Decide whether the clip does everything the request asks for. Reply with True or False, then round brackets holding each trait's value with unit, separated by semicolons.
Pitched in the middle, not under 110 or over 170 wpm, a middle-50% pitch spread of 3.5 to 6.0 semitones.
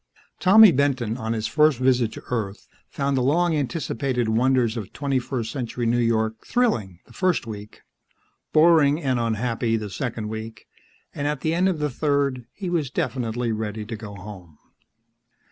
False (125 Hz; 165 wpm; 4.4 semitones)